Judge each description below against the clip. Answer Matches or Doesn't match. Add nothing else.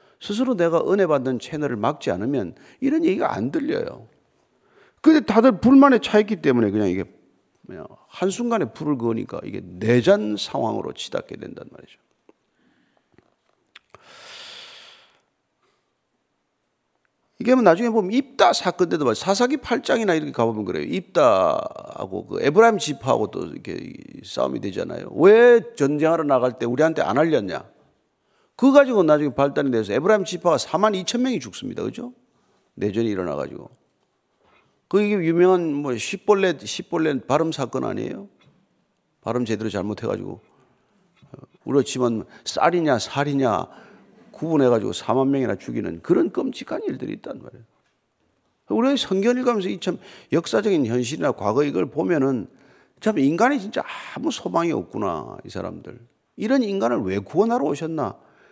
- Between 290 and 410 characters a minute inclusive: Matches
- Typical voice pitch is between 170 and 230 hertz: Matches